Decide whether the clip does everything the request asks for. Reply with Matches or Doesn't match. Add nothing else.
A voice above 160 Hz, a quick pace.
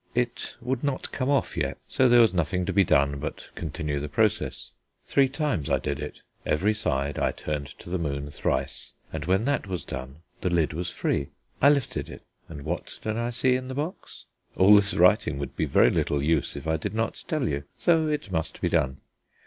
Doesn't match